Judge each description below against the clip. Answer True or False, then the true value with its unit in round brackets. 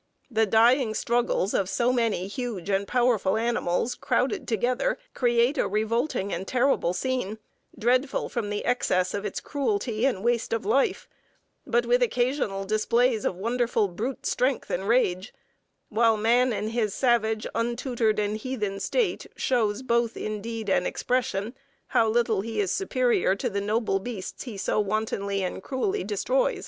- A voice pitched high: True (230 Hz)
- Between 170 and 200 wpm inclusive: False (155 wpm)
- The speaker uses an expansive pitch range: False (3.3 semitones)